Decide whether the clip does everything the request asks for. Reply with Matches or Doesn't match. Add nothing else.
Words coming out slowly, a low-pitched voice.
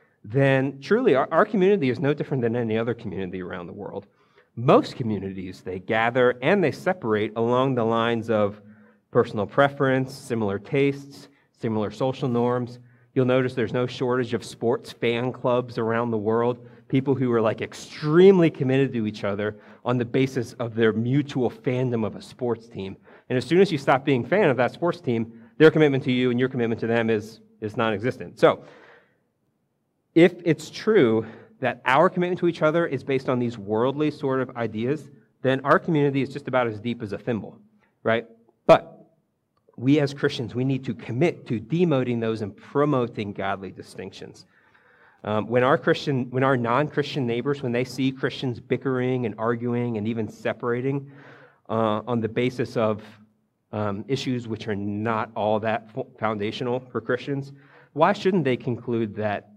Doesn't match